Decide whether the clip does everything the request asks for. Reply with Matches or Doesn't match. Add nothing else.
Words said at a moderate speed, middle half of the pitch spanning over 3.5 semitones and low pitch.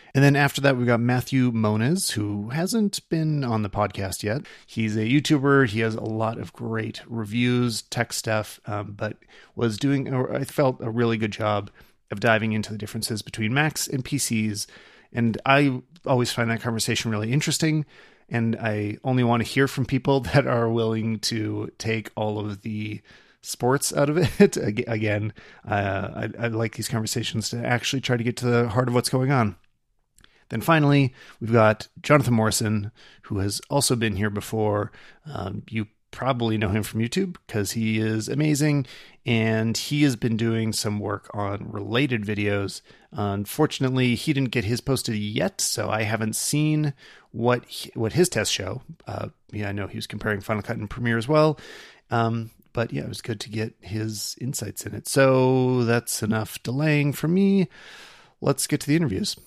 Matches